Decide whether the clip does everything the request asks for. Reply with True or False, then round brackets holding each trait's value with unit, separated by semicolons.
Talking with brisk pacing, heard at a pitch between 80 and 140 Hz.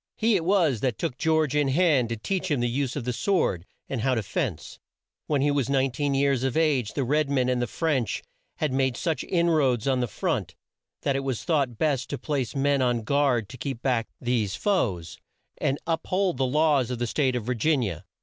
True (230 wpm; 135 Hz)